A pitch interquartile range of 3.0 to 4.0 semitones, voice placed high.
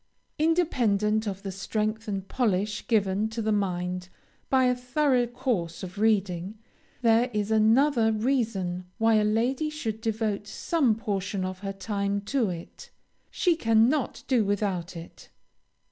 Yes: average, 3.6 semitones; high, 215 Hz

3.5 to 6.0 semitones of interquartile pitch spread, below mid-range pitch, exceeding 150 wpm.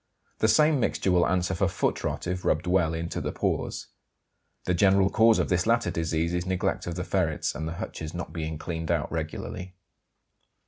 No: narrow, 2.5 semitones; very low, 90 Hz; average, 190 wpm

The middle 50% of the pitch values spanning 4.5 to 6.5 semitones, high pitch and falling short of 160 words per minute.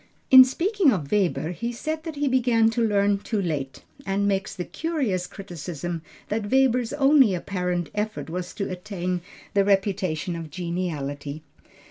Yes: average, 5.2 semitones; high, 195 Hz; average, 150 wpm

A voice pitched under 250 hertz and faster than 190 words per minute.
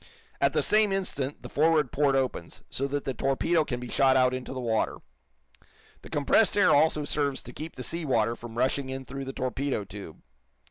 Yes: low, 135 Hz; average, 200 wpm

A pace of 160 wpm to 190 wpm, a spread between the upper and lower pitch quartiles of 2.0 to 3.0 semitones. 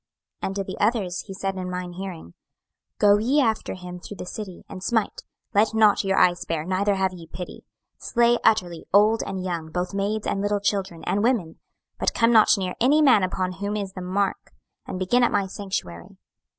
No: fast, 205 wpm; narrow, 2.6 semitones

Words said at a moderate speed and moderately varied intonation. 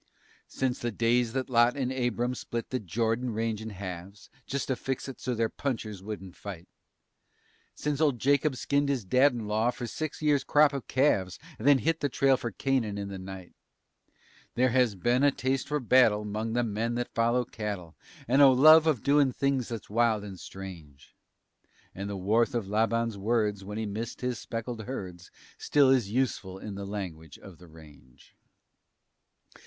Yes: average, 180 wpm; average, 4.3 semitones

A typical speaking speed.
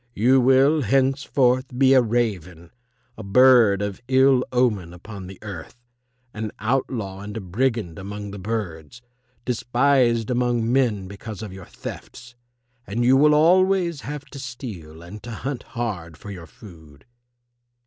Yes: average, 145 wpm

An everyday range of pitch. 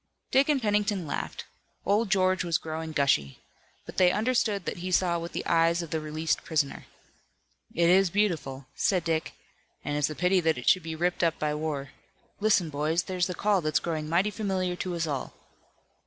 Yes: average, 3.3 semitones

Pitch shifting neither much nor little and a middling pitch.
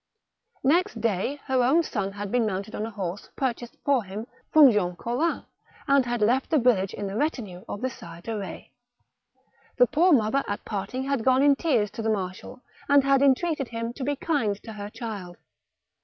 No: average, 5.0 semitones; high, 235 Hz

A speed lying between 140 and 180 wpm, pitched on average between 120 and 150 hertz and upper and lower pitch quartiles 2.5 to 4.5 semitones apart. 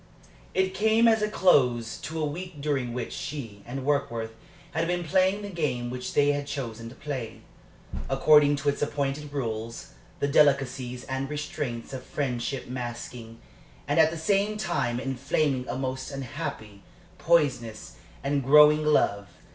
Yes: average, 150 wpm; medium, 140 Hz; average, 3.7 semitones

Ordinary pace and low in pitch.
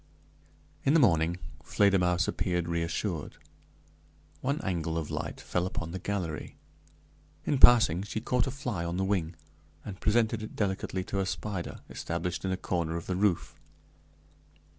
Yes: average, 150 wpm; very low, 95 Hz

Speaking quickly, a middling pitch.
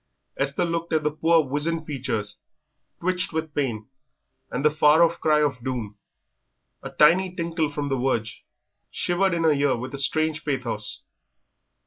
No: average, 155 wpm; medium, 150 Hz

